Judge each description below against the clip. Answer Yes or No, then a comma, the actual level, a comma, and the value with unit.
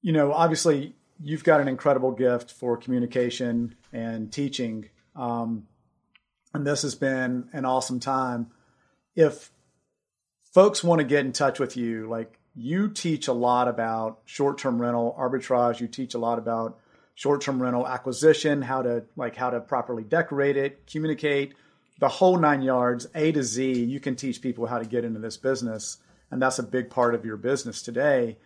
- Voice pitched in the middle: No, low, 125 Hz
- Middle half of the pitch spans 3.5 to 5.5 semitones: No, average, 3.0 semitones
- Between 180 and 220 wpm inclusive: No, average, 170 wpm